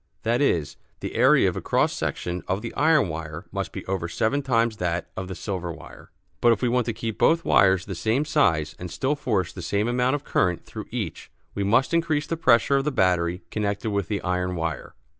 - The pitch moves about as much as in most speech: No, wide, 6.0 semitones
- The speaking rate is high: Yes, fast, 220 wpm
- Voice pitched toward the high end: No, low, 105 Hz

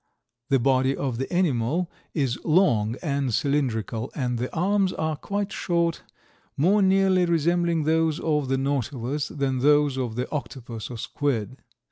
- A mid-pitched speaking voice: Yes, medium, 145 Hz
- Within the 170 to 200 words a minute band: No, average, 145 wpm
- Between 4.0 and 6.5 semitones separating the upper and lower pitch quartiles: Yes, average, 4.9 semitones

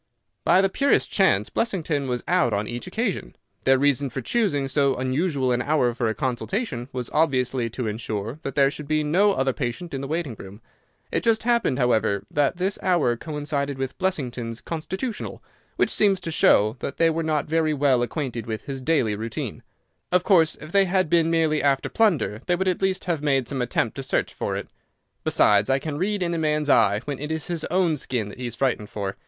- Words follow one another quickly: Yes, fast, 210 wpm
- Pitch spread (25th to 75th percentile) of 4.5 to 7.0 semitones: Yes, wide, 5.6 semitones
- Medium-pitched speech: Yes, medium, 145 Hz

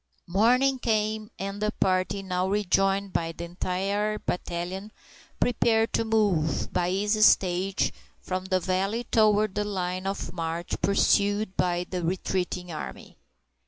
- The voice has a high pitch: Yes, high, 195 Hz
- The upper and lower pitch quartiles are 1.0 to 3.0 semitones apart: Yes, narrow, 2.6 semitones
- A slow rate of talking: Yes, slow, 130 wpm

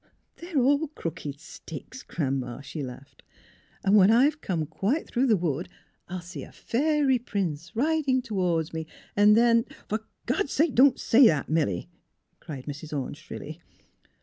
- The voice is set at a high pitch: Yes, high, 200 Hz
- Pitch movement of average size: No, wide, 9.0 semitones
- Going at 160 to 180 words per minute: Yes, average, 175 wpm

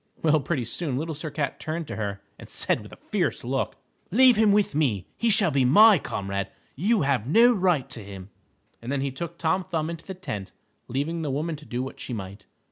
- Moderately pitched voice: Yes, medium, 150 Hz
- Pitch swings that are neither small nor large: No, wide, 5.8 semitones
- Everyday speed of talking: No, fast, 220 wpm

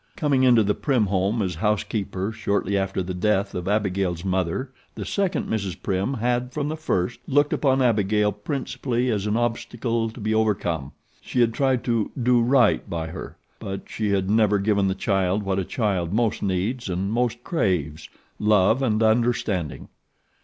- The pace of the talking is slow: No, average, 175 wpm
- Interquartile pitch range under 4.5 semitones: Yes, average, 4.0 semitones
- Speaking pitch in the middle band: No, low, 105 Hz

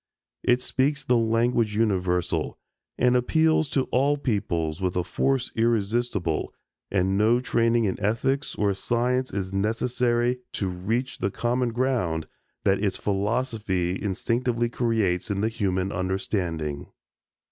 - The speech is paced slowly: Yes, slow, 125 wpm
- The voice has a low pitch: Yes, low, 115 Hz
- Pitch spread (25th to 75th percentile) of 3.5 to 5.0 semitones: Yes, average, 4.4 semitones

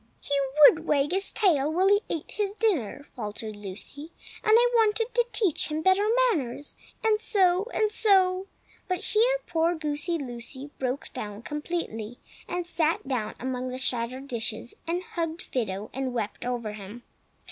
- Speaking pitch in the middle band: No, very high, 300 Hz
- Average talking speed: Yes, average, 155 wpm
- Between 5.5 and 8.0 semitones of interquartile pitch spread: Yes, wide, 7.4 semitones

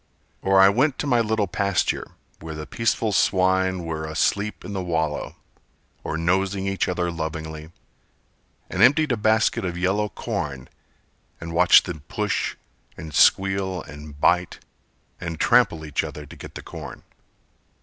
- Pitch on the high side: No, very low, 90 Hz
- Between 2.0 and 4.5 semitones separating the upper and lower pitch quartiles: Yes, average, 4.0 semitones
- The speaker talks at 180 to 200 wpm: No, average, 150 wpm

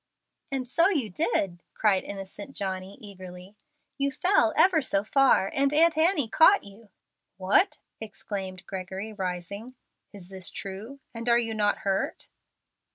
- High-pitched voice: Yes, high, 210 Hz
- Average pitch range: No, wide, 6.1 semitones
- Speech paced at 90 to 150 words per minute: Yes, average, 140 wpm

